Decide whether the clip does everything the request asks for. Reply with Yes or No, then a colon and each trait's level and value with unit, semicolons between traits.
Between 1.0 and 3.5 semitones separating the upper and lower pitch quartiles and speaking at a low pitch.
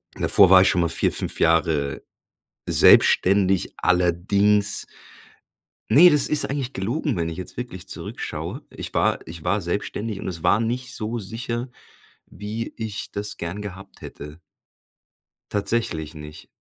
No: average, 4.8 semitones; low, 100 Hz